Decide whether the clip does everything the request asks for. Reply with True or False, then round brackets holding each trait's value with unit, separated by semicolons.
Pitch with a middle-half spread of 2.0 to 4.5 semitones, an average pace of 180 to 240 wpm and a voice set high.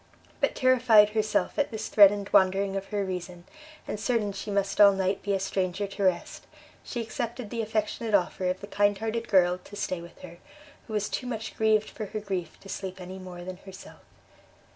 True (2.5 semitones; 200 wpm; 200 Hz)